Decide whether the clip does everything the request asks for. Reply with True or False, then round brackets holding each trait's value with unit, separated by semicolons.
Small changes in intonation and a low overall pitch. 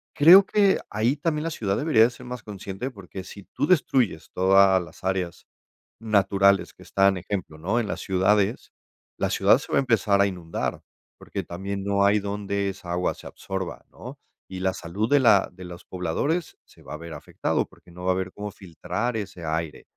False (3.3 semitones; 100 Hz)